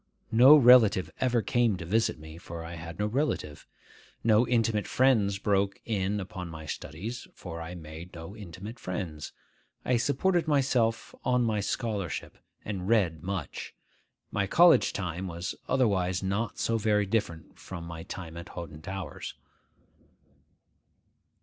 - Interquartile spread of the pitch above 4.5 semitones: Yes, average, 5.1 semitones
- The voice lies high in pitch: No, low, 100 Hz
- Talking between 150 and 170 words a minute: No, average, 140 wpm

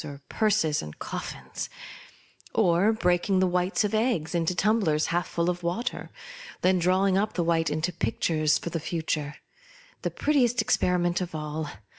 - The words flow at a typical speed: Yes, average, 165 wpm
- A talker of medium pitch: Yes, medium, 175 Hz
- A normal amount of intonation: Yes, average, 4.1 semitones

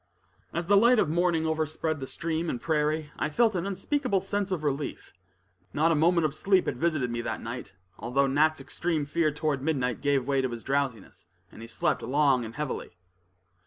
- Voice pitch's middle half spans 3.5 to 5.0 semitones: Yes, average, 3.8 semitones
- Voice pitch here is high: No, medium, 155 Hz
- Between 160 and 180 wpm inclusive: No, average, 195 wpm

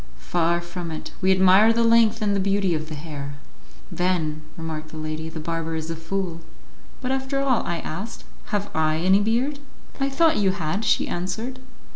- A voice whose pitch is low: No, medium, 185 Hz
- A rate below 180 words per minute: No, average, 185 wpm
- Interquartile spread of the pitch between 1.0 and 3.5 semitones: No, wide, 5.5 semitones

